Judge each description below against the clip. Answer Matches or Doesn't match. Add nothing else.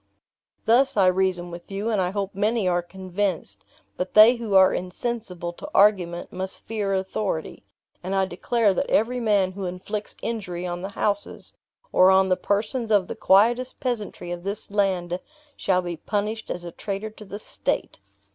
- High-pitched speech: Matches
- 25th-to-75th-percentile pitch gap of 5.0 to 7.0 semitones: Doesn't match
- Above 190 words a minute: Doesn't match